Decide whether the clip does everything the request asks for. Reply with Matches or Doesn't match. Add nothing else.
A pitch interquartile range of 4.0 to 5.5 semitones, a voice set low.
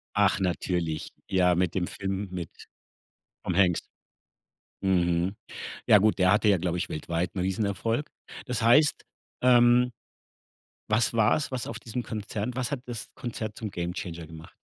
Matches